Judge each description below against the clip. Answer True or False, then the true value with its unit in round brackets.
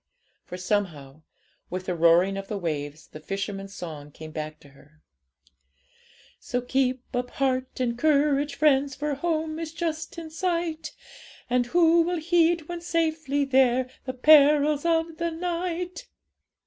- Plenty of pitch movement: True (8.7 semitones)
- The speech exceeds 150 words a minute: False (145 wpm)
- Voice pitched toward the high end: True (275 Hz)